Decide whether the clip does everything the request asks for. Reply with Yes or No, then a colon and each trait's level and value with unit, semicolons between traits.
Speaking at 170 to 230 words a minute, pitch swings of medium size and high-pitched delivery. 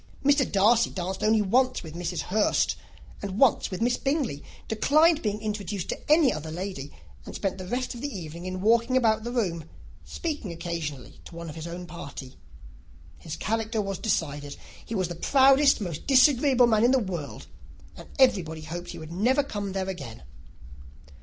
No: average, 180 wpm; wide, 6.2 semitones; high, 200 Hz